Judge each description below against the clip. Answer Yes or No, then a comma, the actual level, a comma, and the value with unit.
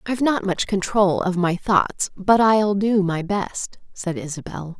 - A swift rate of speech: No, average, 175 wpm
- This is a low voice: No, high, 195 Hz